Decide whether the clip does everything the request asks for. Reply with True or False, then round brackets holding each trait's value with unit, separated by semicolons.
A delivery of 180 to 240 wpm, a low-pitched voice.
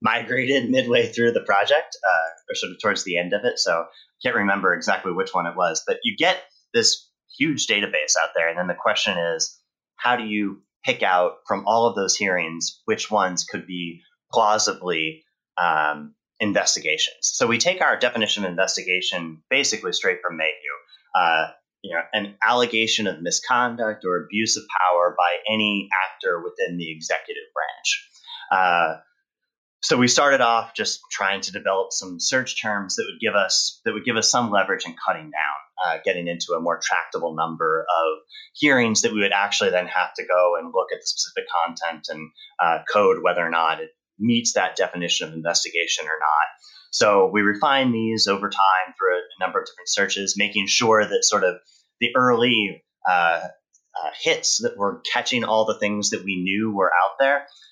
True (185 wpm; 115 Hz)